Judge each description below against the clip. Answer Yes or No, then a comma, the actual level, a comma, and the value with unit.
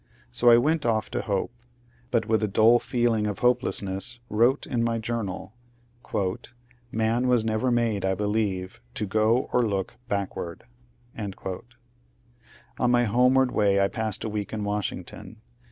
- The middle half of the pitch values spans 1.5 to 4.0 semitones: Yes, average, 2.8 semitones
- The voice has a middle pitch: No, low, 110 Hz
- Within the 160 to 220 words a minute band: No, average, 150 wpm